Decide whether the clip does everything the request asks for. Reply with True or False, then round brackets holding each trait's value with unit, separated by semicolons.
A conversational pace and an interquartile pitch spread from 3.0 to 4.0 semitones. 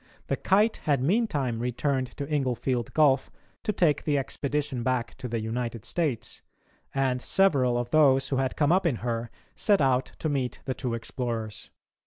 True (170 wpm; 3.4 semitones)